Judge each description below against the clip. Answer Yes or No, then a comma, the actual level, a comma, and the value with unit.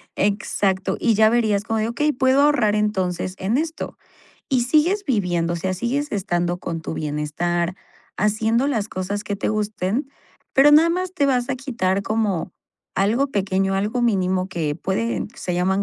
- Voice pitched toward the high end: Yes, high, 210 Hz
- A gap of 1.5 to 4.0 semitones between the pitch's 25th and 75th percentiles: No, average, 4.9 semitones